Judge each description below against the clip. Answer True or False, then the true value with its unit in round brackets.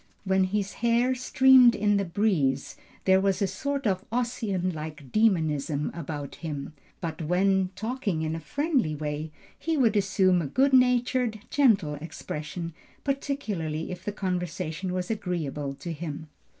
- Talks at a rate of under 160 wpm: True (145 wpm)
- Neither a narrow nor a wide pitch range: False (6.1 semitones)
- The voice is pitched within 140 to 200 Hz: True (185 Hz)